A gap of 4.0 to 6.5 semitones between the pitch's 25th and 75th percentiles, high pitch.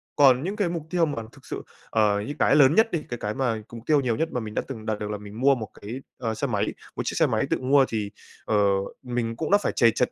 No: average, 4.8 semitones; low, 125 Hz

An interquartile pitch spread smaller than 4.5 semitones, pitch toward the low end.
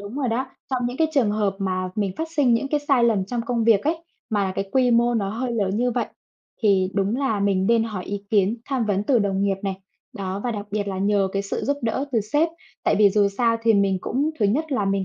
No: average, 3.7 semitones; high, 215 Hz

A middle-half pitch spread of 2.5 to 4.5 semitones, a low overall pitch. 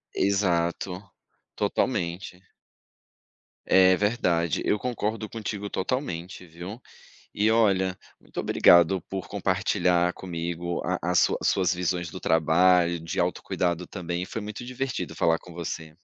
Yes: average, 2.9 semitones; very low, 90 Hz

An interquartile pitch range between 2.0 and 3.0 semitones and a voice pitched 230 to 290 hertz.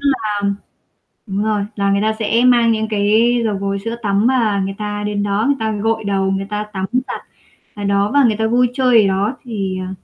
No: narrow, 2.5 semitones; high, 210 Hz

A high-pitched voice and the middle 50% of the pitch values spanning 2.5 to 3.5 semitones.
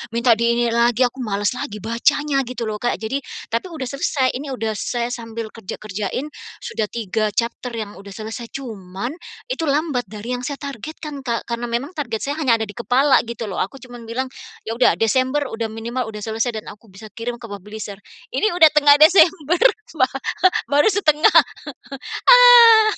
No: high, 240 Hz; average, 4.3 semitones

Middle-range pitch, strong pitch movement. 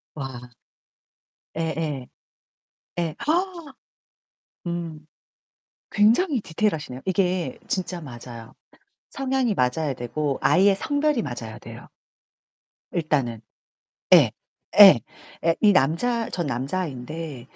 Yes: medium, 165 Hz; wide, 7.8 semitones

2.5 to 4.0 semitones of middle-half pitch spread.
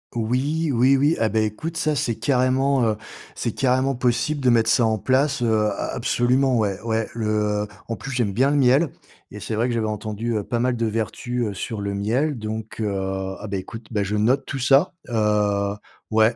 Yes: average, 3.4 semitones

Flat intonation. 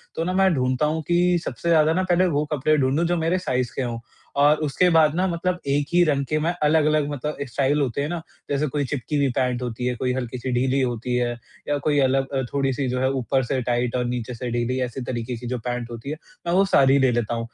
No: average, 3.7 semitones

